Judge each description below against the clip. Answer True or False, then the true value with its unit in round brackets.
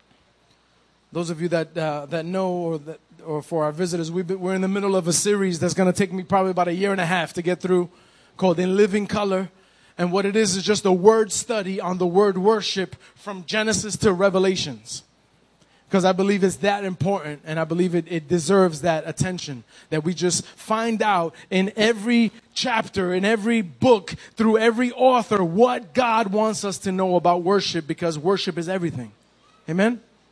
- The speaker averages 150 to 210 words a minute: True (195 wpm)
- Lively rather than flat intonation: False (3.1 semitones)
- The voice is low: False (190 Hz)